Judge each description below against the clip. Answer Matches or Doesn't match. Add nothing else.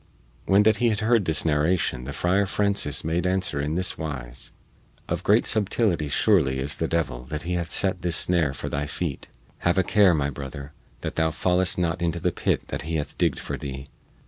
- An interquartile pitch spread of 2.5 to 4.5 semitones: Matches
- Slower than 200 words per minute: Doesn't match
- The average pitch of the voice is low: Matches